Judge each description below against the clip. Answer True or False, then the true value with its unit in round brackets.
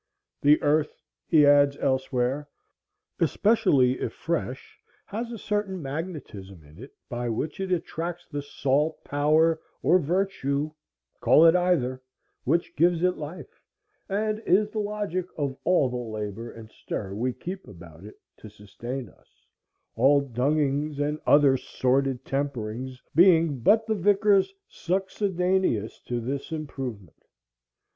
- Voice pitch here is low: False (145 Hz)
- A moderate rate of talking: False (130 wpm)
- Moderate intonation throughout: False (6.1 semitones)